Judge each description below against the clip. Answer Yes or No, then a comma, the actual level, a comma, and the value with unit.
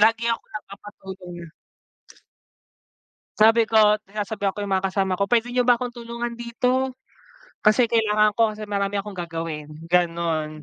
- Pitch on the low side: No, high, 210 Hz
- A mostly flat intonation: No, average, 3.6 semitones